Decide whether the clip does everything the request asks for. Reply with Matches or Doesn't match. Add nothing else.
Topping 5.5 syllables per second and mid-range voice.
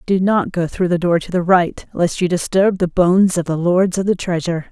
Doesn't match